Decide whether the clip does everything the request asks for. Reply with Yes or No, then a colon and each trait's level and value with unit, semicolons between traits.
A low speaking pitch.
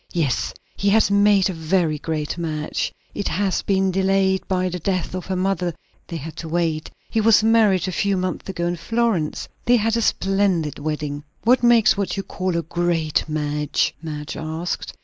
No: medium, 185 Hz